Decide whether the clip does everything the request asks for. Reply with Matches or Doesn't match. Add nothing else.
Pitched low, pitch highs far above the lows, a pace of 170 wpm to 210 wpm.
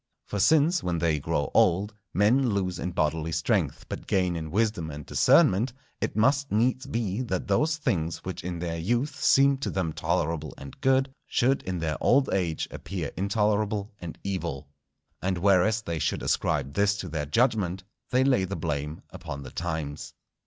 Matches